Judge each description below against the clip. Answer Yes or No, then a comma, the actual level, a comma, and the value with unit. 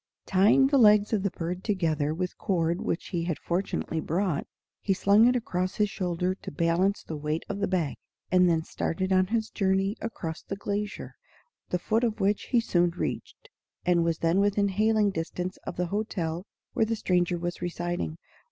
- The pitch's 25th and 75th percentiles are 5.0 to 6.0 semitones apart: No, average, 3.2 semitones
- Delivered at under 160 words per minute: No, average, 185 wpm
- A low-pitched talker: No, medium, 185 Hz